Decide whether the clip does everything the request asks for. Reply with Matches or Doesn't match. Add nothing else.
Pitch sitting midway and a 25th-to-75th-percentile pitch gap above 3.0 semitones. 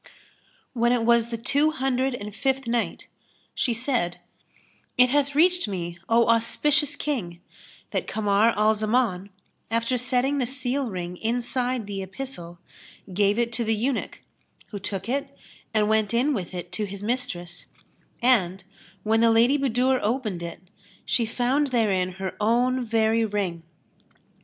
Doesn't match